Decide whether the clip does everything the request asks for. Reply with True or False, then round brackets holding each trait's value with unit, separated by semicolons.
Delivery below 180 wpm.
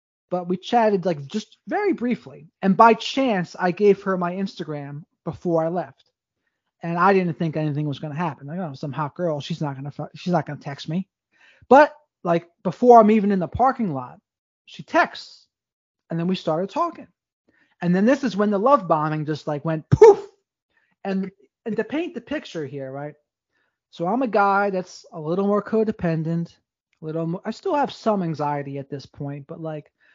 False (200 wpm)